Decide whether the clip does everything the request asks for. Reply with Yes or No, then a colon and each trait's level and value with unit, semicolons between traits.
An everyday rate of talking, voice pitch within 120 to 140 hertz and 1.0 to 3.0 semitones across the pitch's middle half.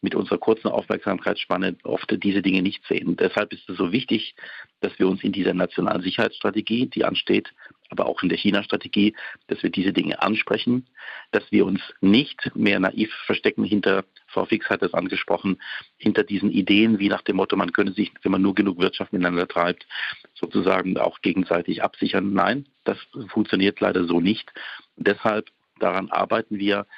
No: average, 175 wpm; low, 100 Hz; narrow, 2.4 semitones